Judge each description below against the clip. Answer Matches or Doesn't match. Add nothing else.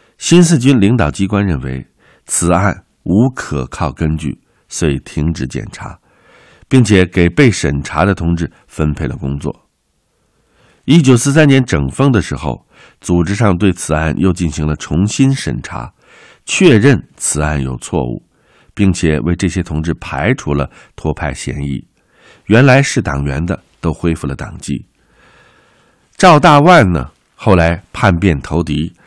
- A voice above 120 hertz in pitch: Doesn't match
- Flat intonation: Doesn't match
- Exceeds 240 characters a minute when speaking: Doesn't match